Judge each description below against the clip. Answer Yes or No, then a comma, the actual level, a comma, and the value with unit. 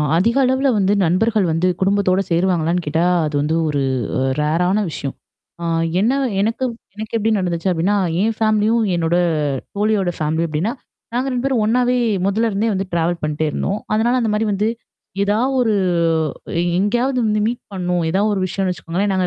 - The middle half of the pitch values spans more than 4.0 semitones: Yes, average, 4.4 semitones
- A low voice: No, high, 200 Hz